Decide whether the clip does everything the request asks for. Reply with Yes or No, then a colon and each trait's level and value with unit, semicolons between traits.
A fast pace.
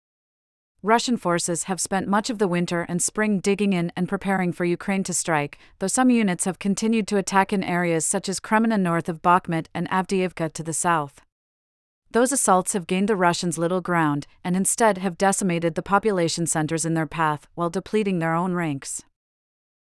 No: average, 185 wpm